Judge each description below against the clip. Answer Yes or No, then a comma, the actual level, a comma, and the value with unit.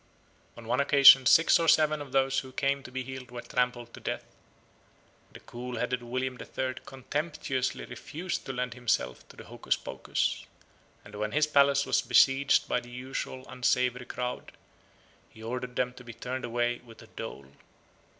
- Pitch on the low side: Yes, low, 125 Hz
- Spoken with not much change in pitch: Yes, narrow, 1.8 semitones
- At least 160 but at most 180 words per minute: Yes, average, 170 wpm